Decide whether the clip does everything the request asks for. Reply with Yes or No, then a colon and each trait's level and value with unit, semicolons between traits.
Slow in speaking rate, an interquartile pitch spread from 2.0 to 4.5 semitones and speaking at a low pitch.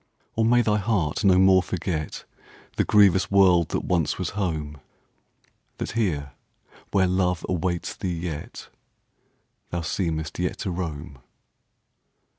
Yes: slow, 110 wpm; average, 3.2 semitones; very low, 90 Hz